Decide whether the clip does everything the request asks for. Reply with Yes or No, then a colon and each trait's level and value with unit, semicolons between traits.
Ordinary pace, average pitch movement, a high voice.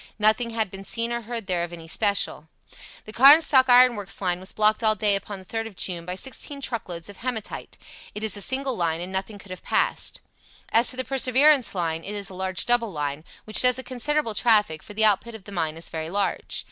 No: fast, 230 wpm; average, 4.5 semitones; high, 210 Hz